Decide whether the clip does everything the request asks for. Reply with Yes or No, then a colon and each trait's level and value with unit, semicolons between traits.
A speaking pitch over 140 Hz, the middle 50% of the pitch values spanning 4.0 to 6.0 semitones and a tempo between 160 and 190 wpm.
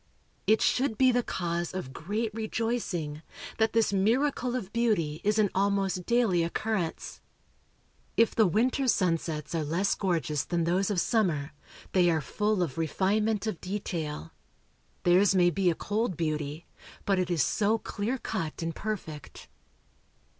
No: high, 190 Hz; average, 4.6 semitones; average, 145 wpm